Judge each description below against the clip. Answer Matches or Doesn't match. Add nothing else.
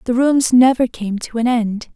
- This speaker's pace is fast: Matches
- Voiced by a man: Doesn't match